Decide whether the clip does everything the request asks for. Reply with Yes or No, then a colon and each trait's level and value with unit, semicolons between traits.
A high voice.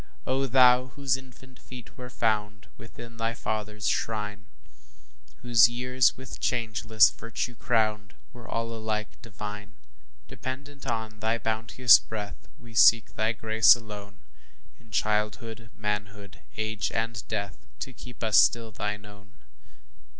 No: low, 110 Hz